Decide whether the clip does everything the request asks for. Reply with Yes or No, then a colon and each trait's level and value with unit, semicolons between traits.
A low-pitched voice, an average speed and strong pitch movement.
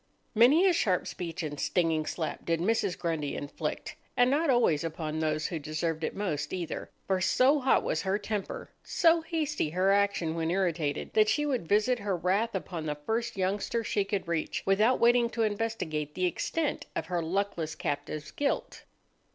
No: high, 190 Hz; average, 175 wpm; wide, 6.0 semitones